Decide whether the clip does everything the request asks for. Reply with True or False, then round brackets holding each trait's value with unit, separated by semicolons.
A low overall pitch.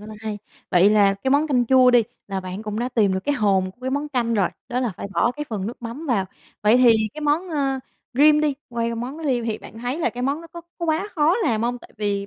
False (245 Hz)